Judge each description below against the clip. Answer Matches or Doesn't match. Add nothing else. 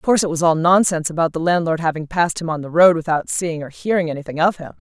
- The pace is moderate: Doesn't match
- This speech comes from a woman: Matches